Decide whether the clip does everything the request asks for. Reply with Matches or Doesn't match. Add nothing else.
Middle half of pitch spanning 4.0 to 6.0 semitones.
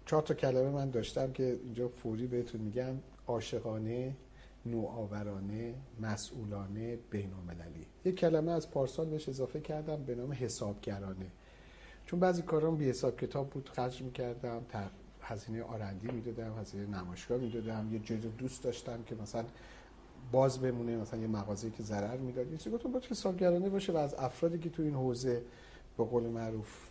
Doesn't match